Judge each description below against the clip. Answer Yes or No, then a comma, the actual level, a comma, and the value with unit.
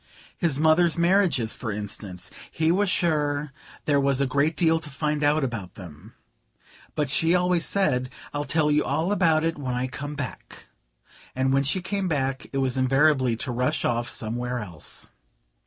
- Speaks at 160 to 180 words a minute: Yes, average, 170 wpm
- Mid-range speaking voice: Yes, medium, 145 Hz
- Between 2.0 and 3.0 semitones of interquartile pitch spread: No, average, 4.3 semitones